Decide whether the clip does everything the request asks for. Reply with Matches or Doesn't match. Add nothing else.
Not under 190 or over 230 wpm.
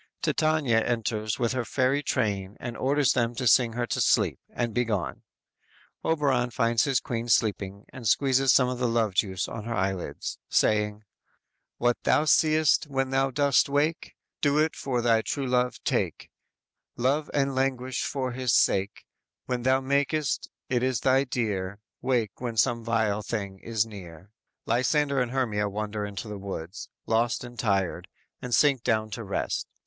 Doesn't match